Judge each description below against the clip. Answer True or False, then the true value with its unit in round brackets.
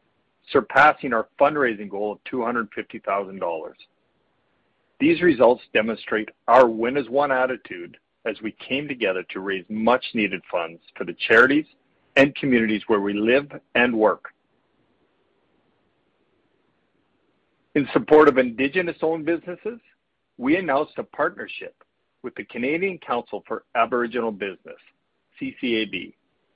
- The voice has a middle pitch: False (125 Hz)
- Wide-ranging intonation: True (7.1 semitones)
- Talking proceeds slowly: True (115 wpm)